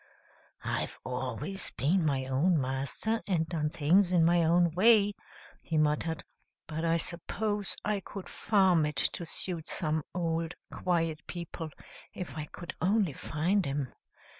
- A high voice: No, medium, 165 Hz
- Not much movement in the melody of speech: No, average, 3.3 semitones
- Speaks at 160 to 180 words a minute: No, average, 140 wpm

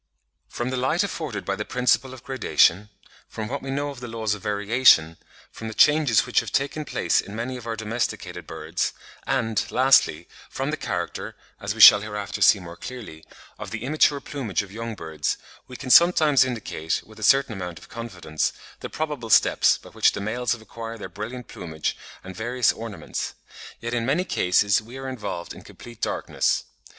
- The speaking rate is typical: Yes, average, 180 wpm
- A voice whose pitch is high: No, low, 115 Hz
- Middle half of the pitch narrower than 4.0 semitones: No, average, 4.3 semitones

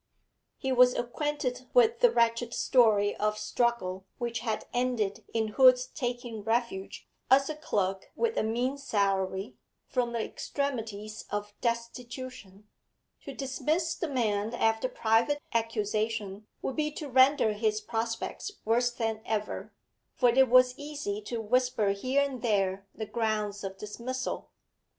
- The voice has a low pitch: No, high, 235 Hz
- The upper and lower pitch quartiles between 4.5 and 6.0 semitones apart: No, average, 3.3 semitones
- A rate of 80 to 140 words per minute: Yes, slow, 135 wpm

